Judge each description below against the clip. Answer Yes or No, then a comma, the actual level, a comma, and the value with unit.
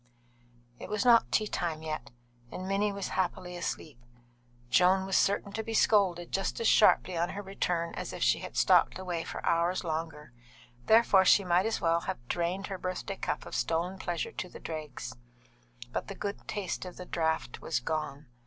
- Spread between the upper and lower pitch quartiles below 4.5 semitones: Yes, average, 3.0 semitones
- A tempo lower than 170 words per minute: No, average, 185 wpm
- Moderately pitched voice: Yes, medium, 180 Hz